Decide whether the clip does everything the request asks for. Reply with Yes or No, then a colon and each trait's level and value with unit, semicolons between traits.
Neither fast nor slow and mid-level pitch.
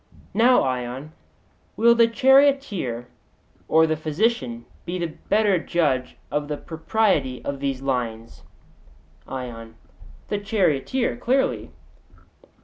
No: slow, 105 wpm; medium, 155 Hz